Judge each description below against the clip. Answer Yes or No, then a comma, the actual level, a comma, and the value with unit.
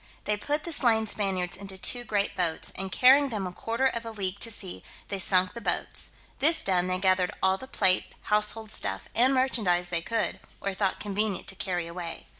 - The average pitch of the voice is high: Yes, high, 200 Hz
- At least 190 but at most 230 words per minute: Yes, fast, 205 wpm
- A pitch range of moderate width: Yes, average, 3.8 semitones